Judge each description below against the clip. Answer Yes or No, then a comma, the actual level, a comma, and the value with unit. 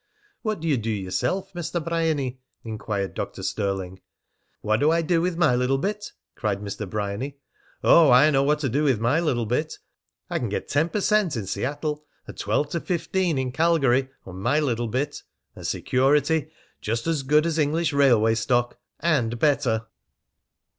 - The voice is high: No, medium, 140 Hz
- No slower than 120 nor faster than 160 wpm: No, average, 170 wpm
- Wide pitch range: Yes, wide, 5.9 semitones